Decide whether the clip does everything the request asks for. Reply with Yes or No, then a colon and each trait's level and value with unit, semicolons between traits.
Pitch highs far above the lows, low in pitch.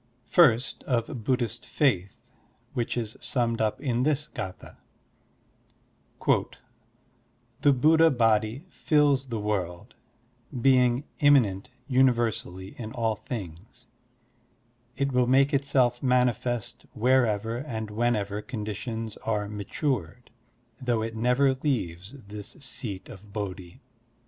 No: average, 3.7 semitones; low, 120 Hz